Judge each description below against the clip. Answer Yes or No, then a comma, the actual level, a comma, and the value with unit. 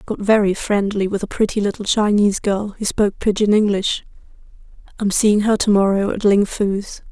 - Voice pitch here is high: Yes, high, 205 Hz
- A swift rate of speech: No, average, 175 wpm